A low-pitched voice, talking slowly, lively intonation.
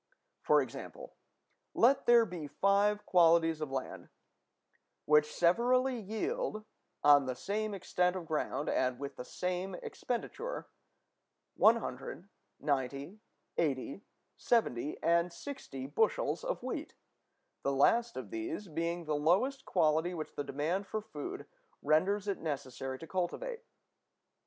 No: medium, 180 Hz; slow, 125 wpm; wide, 6.7 semitones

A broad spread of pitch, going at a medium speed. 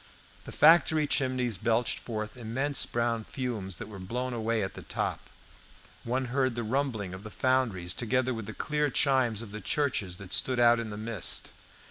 No: average, 3.2 semitones; average, 180 wpm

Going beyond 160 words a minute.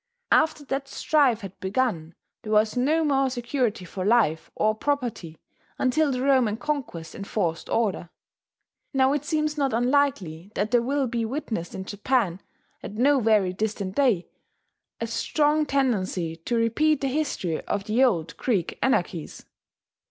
No: average, 145 wpm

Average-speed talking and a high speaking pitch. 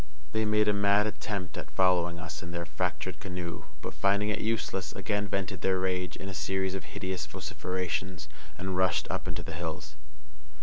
No: average, 180 wpm; very low, 95 Hz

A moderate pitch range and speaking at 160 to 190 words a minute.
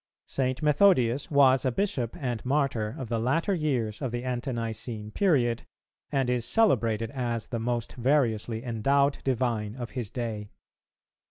No: average, 3.1 semitones; average, 150 wpm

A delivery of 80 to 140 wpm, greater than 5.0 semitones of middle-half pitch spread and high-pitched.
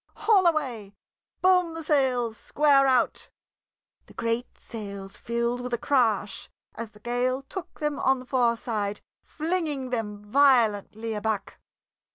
No: slow, 135 wpm; average, 4.3 semitones; high, 245 Hz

